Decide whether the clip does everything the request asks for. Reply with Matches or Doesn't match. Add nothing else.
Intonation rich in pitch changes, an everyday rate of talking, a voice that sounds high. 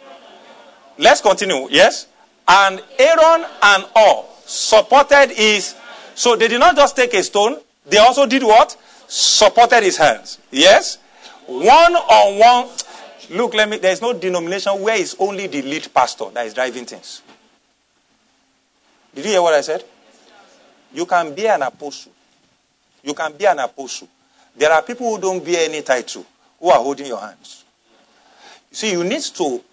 Matches